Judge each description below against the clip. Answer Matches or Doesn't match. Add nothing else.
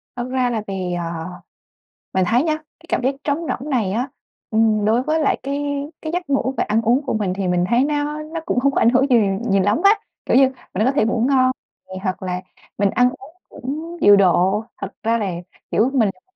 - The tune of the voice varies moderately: Doesn't match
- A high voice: Matches